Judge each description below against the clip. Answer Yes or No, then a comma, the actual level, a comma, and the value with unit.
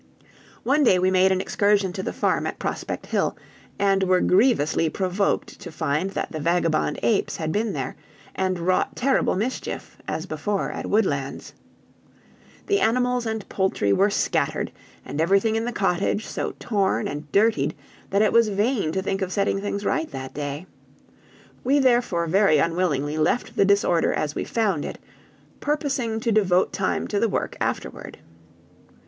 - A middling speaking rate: Yes, average, 165 wpm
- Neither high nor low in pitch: No, high, 195 Hz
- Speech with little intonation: No, average, 4.5 semitones